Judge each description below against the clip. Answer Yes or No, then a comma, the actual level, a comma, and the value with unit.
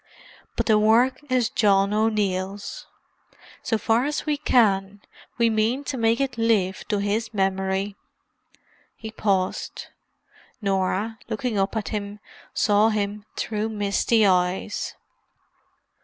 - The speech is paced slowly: Yes, slow, 120 wpm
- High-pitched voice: Yes, high, 210 Hz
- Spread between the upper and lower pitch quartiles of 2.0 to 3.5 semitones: Yes, narrow, 2.4 semitones